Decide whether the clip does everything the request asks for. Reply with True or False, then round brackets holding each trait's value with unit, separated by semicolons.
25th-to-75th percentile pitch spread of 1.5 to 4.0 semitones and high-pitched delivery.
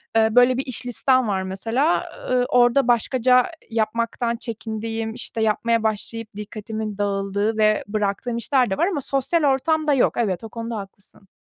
True (2.8 semitones; 230 Hz)